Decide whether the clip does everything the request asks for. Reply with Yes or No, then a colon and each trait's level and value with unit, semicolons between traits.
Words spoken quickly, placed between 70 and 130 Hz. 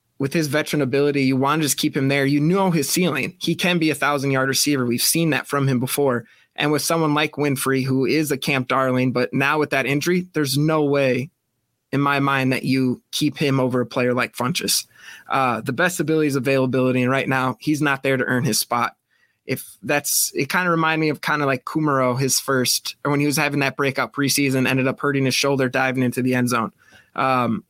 No: fast, 230 wpm; medium, 140 Hz